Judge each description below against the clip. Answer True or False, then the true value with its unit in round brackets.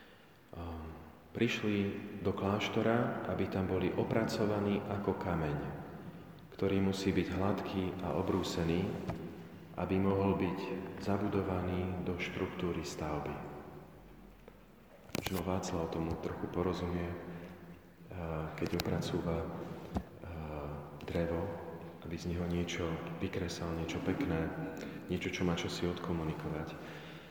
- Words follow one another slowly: True (95 wpm)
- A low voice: True (90 Hz)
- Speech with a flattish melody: True (2.3 semitones)